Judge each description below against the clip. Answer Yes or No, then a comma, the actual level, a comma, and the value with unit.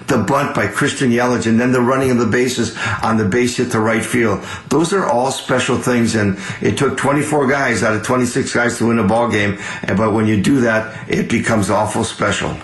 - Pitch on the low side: Yes, low, 120 Hz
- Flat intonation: Yes, narrow, 2.3 semitones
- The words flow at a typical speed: No, fast, 225 wpm